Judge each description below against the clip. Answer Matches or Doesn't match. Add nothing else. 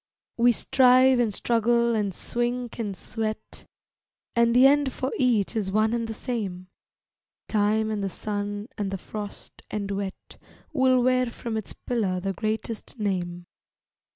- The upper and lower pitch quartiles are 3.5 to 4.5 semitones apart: Doesn't match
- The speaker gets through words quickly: Doesn't match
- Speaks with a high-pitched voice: Matches